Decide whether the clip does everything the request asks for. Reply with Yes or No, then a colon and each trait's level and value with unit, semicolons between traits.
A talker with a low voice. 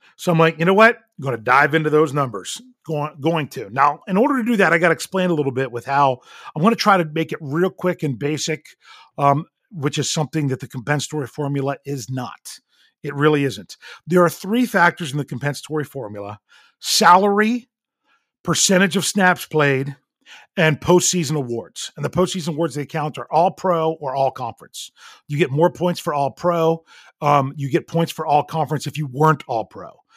No: medium, 155 Hz